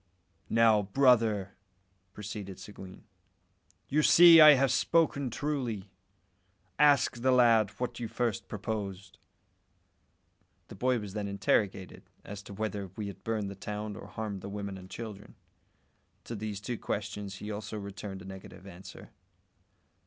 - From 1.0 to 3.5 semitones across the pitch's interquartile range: Yes, average, 3.1 semitones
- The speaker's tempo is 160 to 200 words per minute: No, average, 140 wpm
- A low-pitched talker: Yes, low, 105 Hz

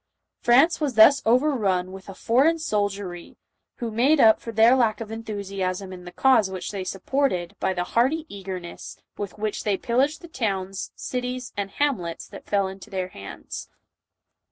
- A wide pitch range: No, average, 4.9 semitones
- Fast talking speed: No, average, 170 wpm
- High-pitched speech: Yes, high, 215 Hz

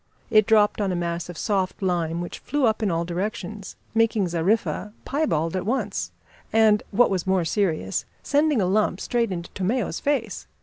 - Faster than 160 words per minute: Yes, average, 175 wpm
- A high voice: Yes, high, 200 Hz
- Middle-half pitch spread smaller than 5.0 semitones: Yes, average, 4.0 semitones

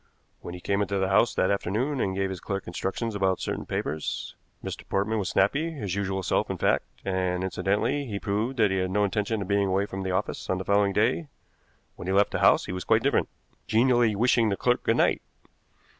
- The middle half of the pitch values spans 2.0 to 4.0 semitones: Yes, narrow, 2.6 semitones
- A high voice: No, low, 100 Hz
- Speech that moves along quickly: Yes, fast, 220 wpm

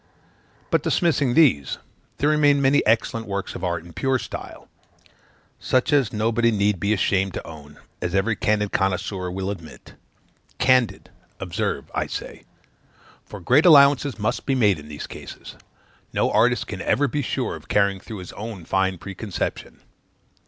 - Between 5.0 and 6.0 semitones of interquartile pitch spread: Yes, wide, 5.4 semitones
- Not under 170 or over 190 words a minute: No, average, 160 wpm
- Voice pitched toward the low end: Yes, low, 105 Hz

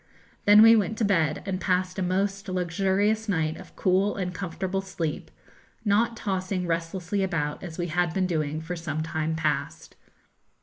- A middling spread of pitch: Yes, average, 3.1 semitones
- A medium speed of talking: Yes, average, 165 wpm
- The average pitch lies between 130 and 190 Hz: Yes, medium, 185 Hz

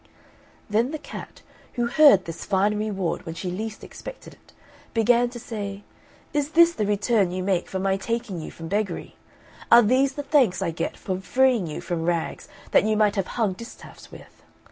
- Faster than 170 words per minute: Yes, average, 190 wpm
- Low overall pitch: No, high, 210 Hz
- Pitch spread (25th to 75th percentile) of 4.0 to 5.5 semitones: Yes, average, 4.3 semitones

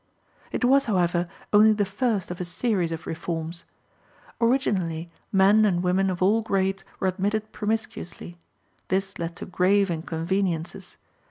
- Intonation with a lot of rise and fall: No, average, 3.1 semitones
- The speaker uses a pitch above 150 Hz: Yes, high, 190 Hz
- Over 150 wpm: No, average, 140 wpm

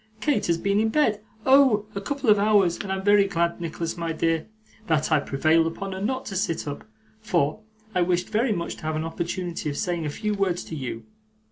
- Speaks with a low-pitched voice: No, medium, 180 Hz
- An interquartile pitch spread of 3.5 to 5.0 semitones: Yes, average, 4.1 semitones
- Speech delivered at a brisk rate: Yes, fast, 220 wpm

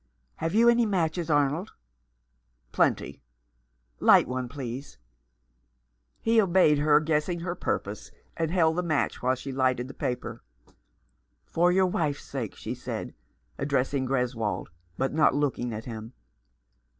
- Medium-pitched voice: Yes, medium, 145 Hz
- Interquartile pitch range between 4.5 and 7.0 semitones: Yes, average, 5.1 semitones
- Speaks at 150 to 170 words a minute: No, average, 140 wpm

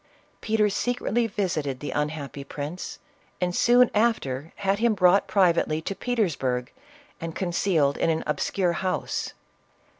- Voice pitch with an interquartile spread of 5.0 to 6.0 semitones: Yes, wide, 5.5 semitones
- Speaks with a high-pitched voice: No, medium, 180 Hz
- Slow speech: Yes, slow, 130 wpm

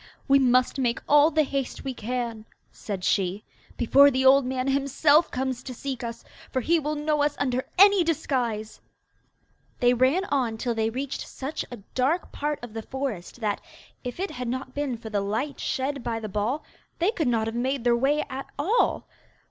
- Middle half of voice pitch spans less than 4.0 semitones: Yes, average, 3.4 semitones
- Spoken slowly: No, average, 190 wpm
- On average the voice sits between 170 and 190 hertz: No, very high, 260 Hz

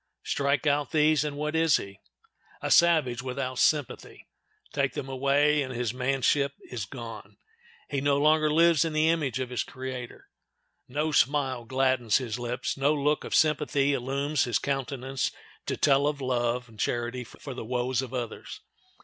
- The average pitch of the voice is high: No, low, 135 Hz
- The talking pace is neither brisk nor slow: Yes, average, 165 wpm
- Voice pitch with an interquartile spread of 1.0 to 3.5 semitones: Yes, average, 2.9 semitones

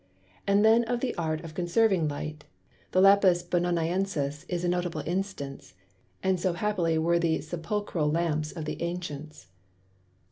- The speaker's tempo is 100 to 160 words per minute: Yes, average, 145 wpm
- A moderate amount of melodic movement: Yes, average, 3.2 semitones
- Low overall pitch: No, medium, 170 Hz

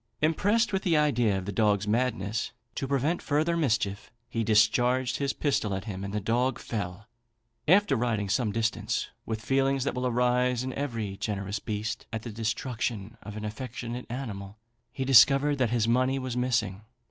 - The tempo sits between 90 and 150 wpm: No, average, 170 wpm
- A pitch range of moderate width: Yes, average, 3.9 semitones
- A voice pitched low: Yes, low, 120 Hz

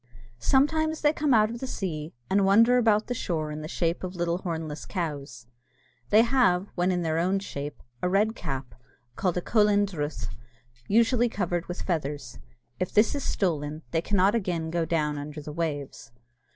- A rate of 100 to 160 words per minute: No, average, 180 wpm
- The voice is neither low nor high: Yes, medium, 180 Hz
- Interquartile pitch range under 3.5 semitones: No, wide, 5.4 semitones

